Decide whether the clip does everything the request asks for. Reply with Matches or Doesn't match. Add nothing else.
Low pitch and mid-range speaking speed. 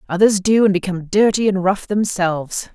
Doesn't match